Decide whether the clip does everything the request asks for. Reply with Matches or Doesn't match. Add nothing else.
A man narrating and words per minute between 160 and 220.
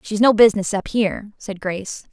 Doesn't match